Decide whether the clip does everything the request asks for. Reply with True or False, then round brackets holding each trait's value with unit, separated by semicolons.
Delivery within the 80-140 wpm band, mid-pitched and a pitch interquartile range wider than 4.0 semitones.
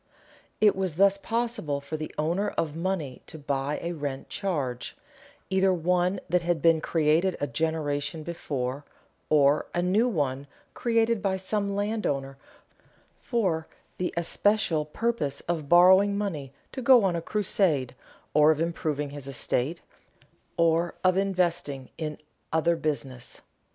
True (135 wpm; 165 Hz; 4.7 semitones)